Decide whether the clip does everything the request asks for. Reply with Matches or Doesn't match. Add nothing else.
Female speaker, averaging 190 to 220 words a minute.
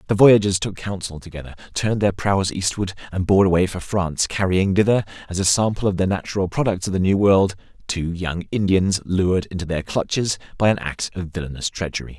Doesn't match